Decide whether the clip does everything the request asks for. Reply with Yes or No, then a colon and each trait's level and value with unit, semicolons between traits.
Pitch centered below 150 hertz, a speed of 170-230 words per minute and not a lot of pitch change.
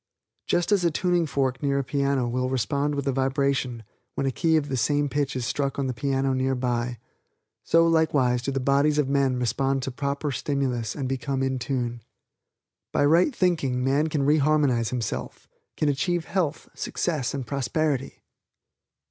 Yes: medium, 140 Hz; average, 175 wpm; narrow, 2.3 semitones